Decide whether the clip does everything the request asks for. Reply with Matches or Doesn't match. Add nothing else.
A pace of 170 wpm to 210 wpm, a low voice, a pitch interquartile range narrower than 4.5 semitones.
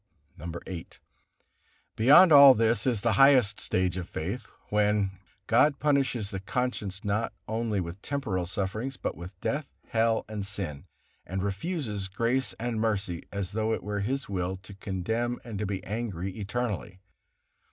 Doesn't match